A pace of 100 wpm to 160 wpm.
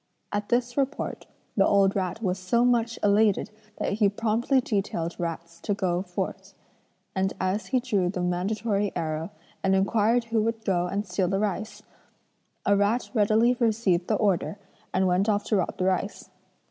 No: average, 170 wpm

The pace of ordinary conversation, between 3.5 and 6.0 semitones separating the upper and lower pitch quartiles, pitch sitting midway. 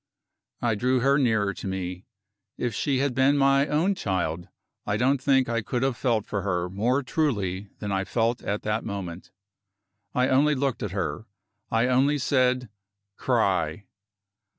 No: average, 160 wpm; average, 5.1 semitones; low, 120 Hz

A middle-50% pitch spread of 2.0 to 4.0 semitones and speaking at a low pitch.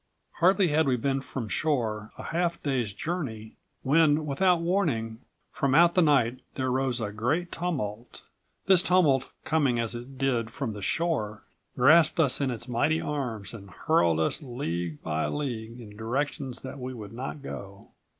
No: wide, 5.4 semitones; low, 130 Hz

